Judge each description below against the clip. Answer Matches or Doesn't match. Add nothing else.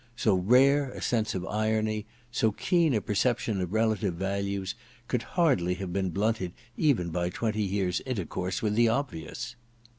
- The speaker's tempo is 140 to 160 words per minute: Matches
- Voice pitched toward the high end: Doesn't match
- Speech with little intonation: Doesn't match